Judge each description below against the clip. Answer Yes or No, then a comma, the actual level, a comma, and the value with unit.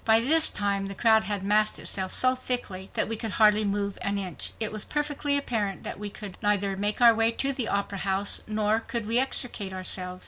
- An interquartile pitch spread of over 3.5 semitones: No, narrow, 2.6 semitones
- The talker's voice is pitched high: Yes, high, 210 Hz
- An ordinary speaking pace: No, fast, 215 wpm